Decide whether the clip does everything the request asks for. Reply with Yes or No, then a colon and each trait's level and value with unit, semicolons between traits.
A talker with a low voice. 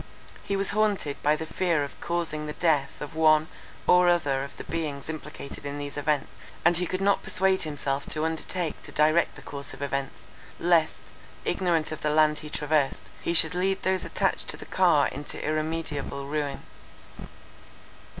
No: medium, 155 Hz